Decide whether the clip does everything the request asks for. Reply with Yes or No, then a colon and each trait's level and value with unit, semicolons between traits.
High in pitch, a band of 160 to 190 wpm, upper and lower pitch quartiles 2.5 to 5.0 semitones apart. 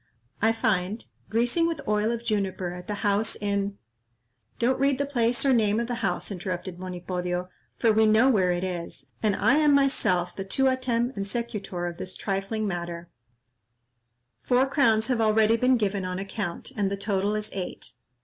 Yes: high, 210 Hz; average, 175 wpm; average, 4.0 semitones